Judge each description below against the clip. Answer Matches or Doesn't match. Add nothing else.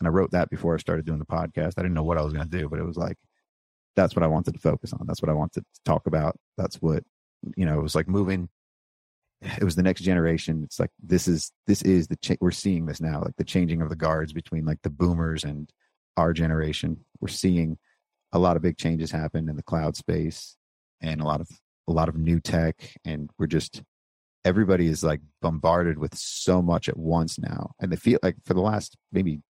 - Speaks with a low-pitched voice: Matches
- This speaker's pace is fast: Matches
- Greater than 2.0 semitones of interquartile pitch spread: Matches